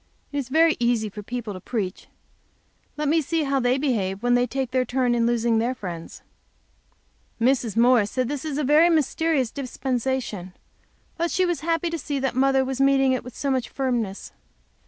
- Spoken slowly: No, average, 190 wpm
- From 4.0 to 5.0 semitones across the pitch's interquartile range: No, average, 3.1 semitones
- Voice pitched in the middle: No, very high, 255 Hz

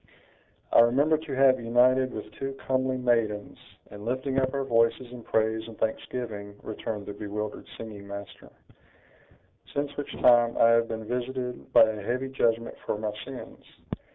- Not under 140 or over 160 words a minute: Yes, average, 155 wpm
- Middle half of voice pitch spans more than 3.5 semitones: No, average, 3.0 semitones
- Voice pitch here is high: No, low, 120 Hz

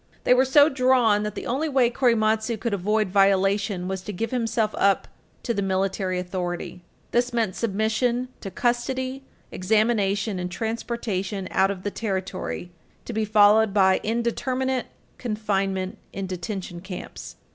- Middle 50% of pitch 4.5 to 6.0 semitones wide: No, average, 3.6 semitones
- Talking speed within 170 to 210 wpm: No, average, 145 wpm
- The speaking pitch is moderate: No, high, 210 Hz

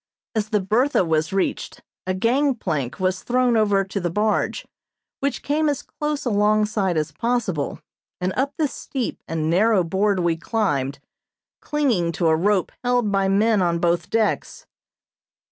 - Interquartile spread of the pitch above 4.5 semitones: Yes, wide, 5.4 semitones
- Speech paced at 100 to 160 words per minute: Yes, average, 150 wpm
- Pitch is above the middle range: Yes, high, 205 Hz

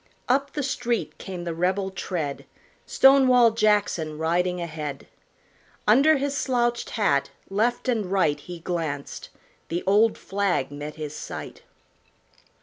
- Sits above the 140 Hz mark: Yes, high, 190 Hz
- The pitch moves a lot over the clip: Yes, wide, 6.7 semitones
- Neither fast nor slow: No, slow, 125 wpm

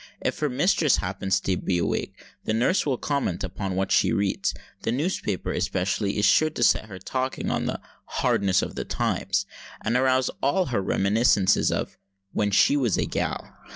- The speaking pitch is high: No, low, 105 Hz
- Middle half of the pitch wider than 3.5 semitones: Yes, average, 5.3 semitones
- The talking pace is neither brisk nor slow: Yes, average, 180 wpm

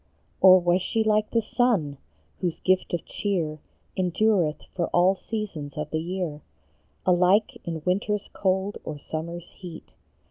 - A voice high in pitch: No, medium, 180 Hz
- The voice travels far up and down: No, average, 3.7 semitones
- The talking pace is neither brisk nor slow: Yes, average, 150 wpm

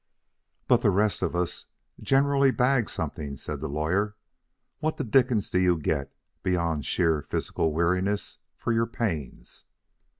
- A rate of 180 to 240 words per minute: No, average, 140 wpm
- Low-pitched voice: Yes, very low, 90 Hz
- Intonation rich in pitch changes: Yes, wide, 6.5 semitones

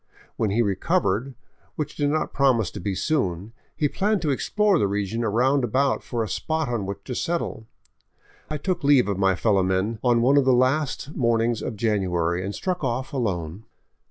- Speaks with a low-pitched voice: Yes, low, 120 Hz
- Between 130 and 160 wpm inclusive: No, average, 185 wpm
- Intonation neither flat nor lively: No, wide, 5.9 semitones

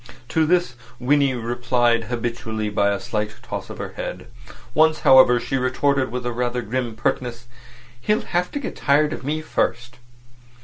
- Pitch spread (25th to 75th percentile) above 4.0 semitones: No, average, 3.2 semitones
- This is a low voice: Yes, low, 125 Hz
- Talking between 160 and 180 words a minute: Yes, average, 165 wpm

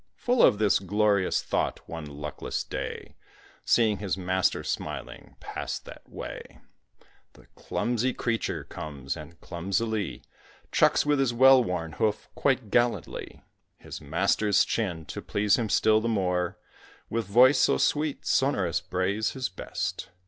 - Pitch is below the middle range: Yes, low, 105 Hz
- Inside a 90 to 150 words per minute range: Yes, slow, 135 wpm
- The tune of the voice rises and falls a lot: No, average, 4.8 semitones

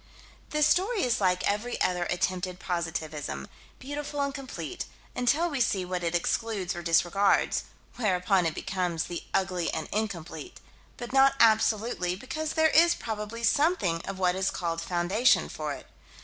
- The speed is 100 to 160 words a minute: Yes, average, 150 wpm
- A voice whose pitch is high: Yes, high, 195 Hz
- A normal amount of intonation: No, wide, 6.0 semitones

